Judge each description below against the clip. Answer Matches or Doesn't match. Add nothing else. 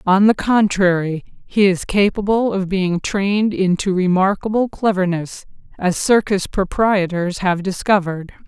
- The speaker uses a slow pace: Matches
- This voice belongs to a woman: Matches